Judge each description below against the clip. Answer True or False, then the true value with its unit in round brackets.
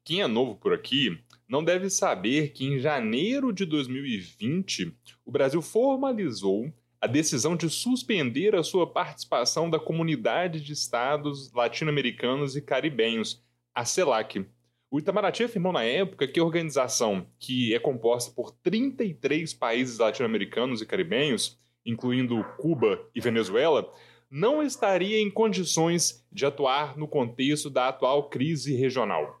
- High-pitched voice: False (150 Hz)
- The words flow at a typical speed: True (135 wpm)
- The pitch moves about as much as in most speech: False (6.7 semitones)